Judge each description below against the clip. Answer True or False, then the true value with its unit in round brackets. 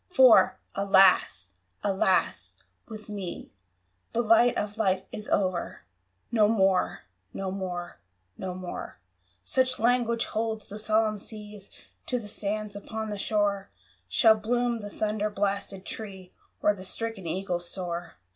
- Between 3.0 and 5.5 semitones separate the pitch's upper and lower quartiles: False (2.5 semitones)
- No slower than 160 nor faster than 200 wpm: False (135 wpm)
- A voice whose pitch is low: False (205 Hz)